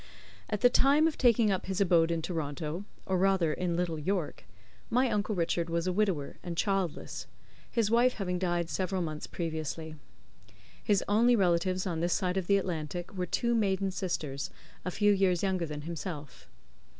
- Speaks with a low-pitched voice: No, medium, 180 Hz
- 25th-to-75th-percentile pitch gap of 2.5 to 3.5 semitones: Yes, average, 3.0 semitones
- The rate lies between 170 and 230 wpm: Yes, average, 175 wpm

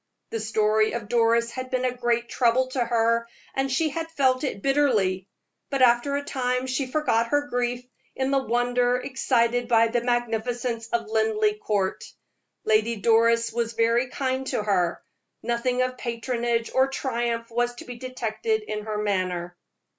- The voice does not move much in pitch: Yes, narrow, 2.1 semitones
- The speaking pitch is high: Yes, high, 240 Hz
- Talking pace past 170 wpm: No, average, 160 wpm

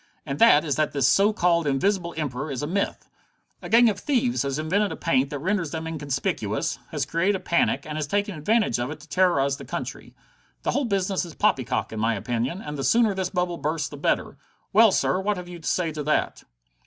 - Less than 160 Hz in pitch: No, medium, 165 Hz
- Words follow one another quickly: Yes, fast, 225 wpm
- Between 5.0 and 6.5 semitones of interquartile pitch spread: Yes, wide, 5.6 semitones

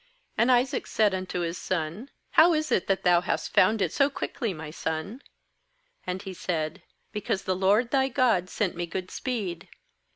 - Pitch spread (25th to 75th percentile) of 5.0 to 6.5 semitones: Yes, average, 5.3 semitones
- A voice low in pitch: No, high, 190 Hz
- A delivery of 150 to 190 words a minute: Yes, average, 175 wpm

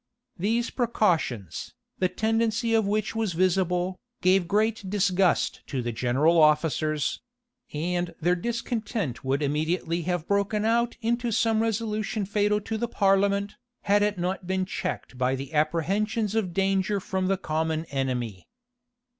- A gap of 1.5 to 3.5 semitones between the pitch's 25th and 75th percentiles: No, average, 4.9 semitones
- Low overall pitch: No, high, 190 Hz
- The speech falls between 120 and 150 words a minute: Yes, average, 140 wpm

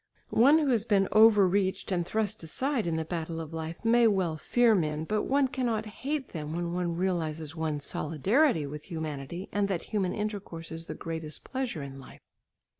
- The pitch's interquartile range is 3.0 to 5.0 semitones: No, wide, 5.4 semitones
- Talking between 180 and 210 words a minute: Yes, average, 185 wpm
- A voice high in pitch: No, medium, 180 Hz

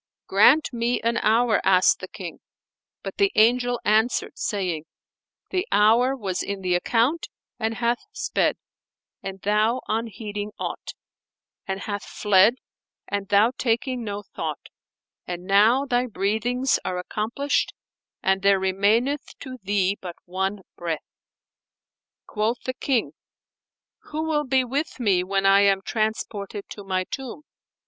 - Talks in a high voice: Yes, high, 215 Hz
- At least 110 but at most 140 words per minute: Yes, slow, 135 wpm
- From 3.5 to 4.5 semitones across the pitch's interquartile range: Yes, average, 3.9 semitones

